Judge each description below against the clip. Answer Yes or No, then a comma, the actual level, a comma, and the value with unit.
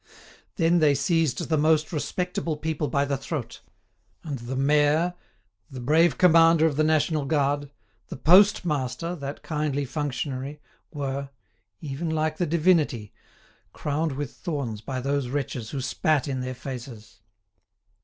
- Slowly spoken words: Yes, slow, 130 wpm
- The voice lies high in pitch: No, medium, 145 Hz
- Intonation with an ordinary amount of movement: Yes, average, 3.0 semitones